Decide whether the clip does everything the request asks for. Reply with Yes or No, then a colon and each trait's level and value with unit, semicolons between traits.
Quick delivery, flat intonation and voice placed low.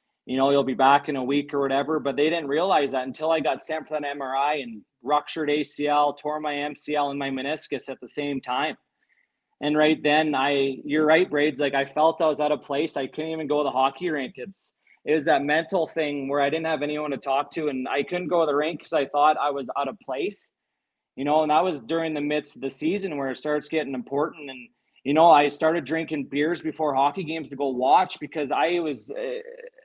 No: fast, 240 wpm; narrow, 2.1 semitones; medium, 150 Hz